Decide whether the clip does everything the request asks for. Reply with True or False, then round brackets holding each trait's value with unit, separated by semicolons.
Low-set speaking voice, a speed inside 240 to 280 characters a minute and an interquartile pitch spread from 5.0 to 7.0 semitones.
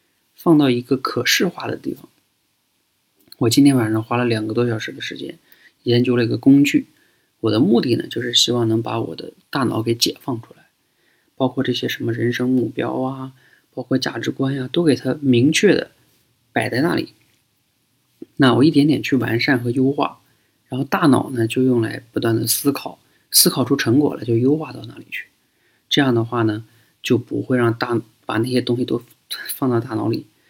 False (125 Hz; 270 characters per minute; 2.7 semitones)